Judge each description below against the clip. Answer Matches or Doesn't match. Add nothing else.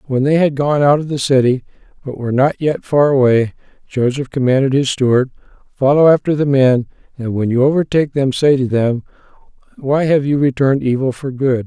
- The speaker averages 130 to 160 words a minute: Doesn't match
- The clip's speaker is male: Matches